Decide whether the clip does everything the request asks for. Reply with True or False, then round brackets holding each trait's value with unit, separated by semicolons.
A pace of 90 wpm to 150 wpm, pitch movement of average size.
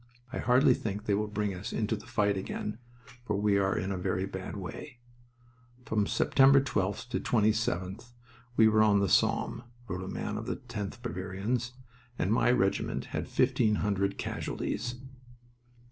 False (160 wpm; 3.2 semitones)